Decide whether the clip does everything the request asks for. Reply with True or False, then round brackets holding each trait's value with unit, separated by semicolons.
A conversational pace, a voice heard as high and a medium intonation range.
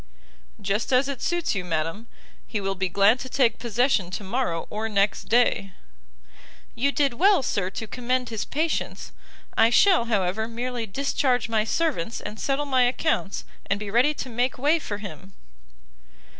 True (165 wpm; 230 Hz; 4.6 semitones)